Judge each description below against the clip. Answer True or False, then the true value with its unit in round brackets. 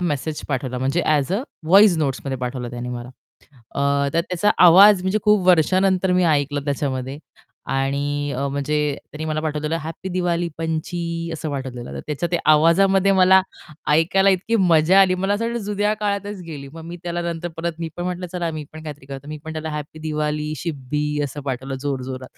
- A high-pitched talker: False (160 Hz)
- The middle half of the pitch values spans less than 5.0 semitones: True (4.2 semitones)